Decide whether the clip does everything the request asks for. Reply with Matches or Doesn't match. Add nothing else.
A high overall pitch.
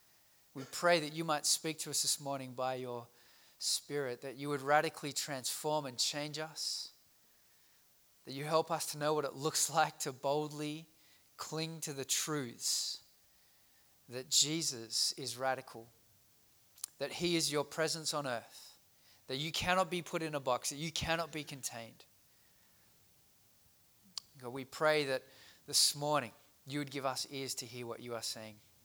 Doesn't match